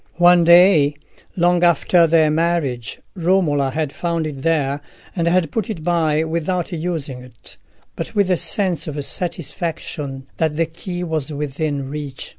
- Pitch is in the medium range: Yes, medium, 160 Hz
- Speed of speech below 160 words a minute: Yes, average, 150 wpm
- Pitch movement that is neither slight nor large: Yes, average, 3.1 semitones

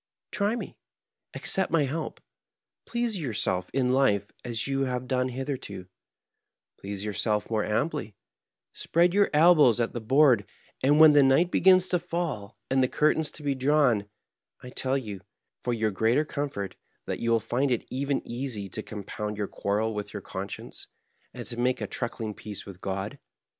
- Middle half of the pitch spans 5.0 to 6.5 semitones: Yes, wide, 5.6 semitones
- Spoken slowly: No, average, 175 wpm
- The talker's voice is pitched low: Yes, low, 125 Hz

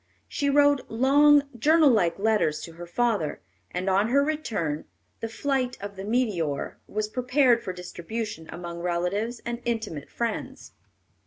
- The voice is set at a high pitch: Yes, high, 220 Hz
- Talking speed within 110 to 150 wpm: Yes, average, 145 wpm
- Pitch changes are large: Yes, wide, 6.1 semitones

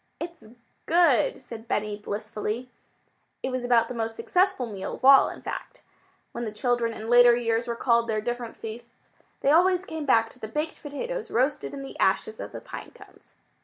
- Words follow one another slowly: No, average, 185 wpm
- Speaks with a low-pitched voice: No, high, 240 Hz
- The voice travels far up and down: No, average, 4.2 semitones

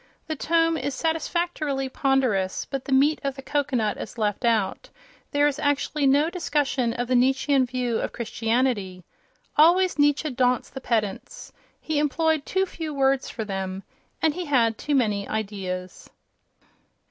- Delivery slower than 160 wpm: Yes, average, 145 wpm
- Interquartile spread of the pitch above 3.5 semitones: Yes, average, 4.5 semitones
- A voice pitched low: No, very high, 270 Hz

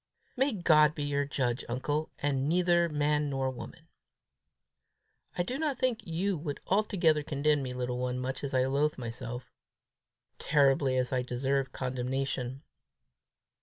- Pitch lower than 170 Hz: Yes, medium, 140 Hz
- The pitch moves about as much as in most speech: Yes, average, 3.3 semitones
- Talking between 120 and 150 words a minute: Yes, average, 140 wpm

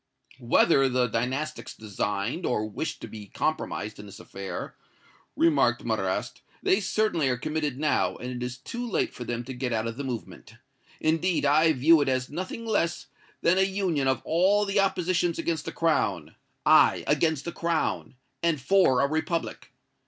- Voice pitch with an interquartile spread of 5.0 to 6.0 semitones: Yes, wide, 5.6 semitones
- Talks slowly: No, average, 170 wpm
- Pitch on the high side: No, medium, 140 Hz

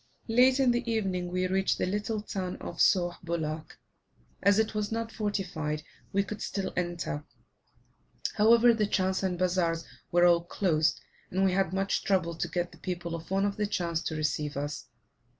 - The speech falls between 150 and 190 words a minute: Yes, average, 180 wpm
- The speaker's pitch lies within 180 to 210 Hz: Yes, medium, 185 Hz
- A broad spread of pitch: No, average, 3.4 semitones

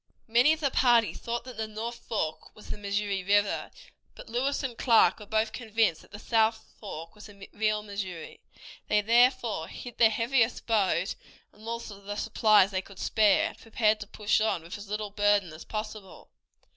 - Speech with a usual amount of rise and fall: No, narrow, 2.2 semitones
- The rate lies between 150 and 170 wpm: No, average, 185 wpm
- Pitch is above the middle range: Yes, high, 215 Hz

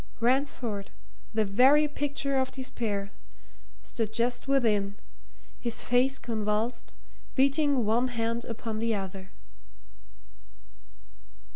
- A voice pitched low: No, high, 235 Hz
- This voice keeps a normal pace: No, slow, 95 wpm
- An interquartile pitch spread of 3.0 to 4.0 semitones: Yes, average, 3.7 semitones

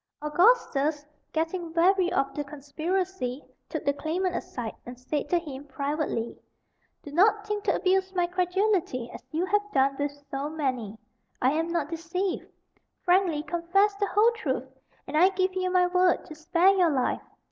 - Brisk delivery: No, average, 165 wpm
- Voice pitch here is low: No, very high, 335 Hz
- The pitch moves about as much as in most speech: Yes, average, 4.5 semitones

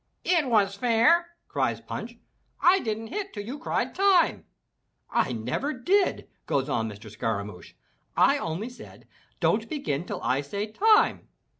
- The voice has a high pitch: Yes, high, 220 Hz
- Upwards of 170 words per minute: No, average, 150 wpm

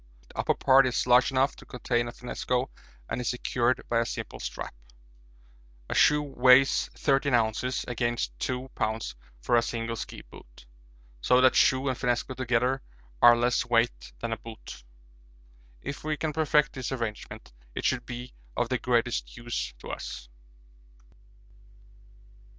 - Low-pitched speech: Yes, low, 125 Hz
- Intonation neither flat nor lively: No, narrow, 1.8 semitones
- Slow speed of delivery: No, average, 150 wpm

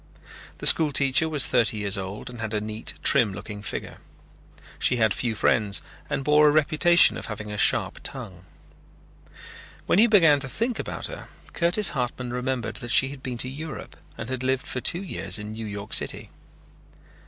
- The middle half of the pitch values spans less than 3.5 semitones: No, wide, 5.6 semitones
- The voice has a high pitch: No, low, 125 Hz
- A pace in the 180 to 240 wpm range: Yes, average, 185 wpm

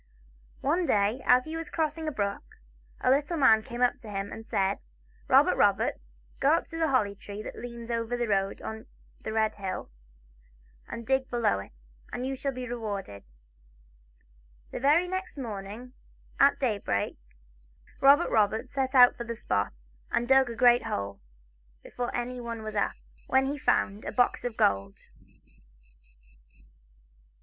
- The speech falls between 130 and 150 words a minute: No, average, 160 wpm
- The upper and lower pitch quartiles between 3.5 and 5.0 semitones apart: Yes, average, 4.6 semitones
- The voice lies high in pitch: Yes, high, 235 Hz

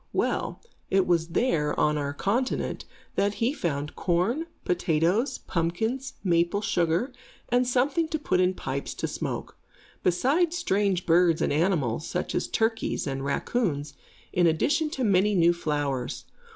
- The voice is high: No, medium, 180 Hz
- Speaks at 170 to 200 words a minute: No, average, 140 wpm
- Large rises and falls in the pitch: Yes, wide, 6.8 semitones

